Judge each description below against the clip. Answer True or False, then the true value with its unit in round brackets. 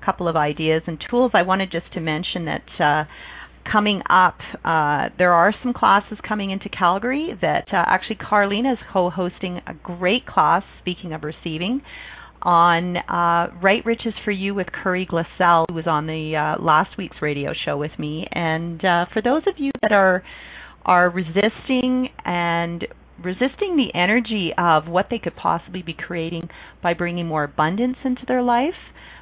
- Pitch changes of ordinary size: True (4.1 semitones)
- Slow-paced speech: False (170 wpm)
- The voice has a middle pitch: True (180 Hz)